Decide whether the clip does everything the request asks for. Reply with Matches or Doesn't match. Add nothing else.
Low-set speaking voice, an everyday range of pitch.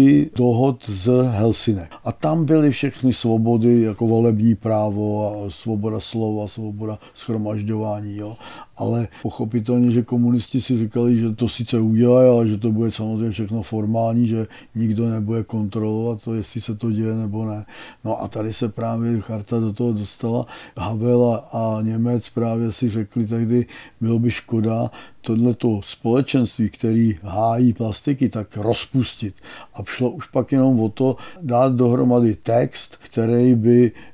Doesn't match